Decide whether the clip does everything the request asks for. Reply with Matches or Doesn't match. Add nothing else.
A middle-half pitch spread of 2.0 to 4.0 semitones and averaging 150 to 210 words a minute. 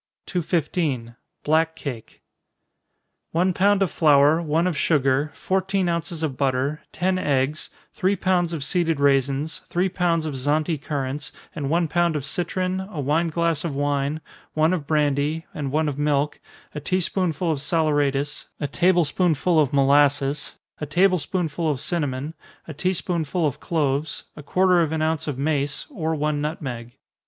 Matches